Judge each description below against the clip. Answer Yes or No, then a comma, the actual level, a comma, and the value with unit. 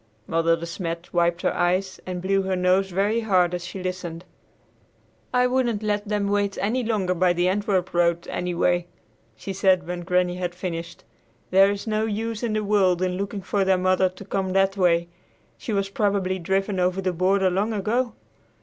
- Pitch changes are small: Yes, narrow, 2.3 semitones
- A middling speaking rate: Yes, average, 185 wpm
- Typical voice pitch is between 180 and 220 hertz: Yes, high, 190 Hz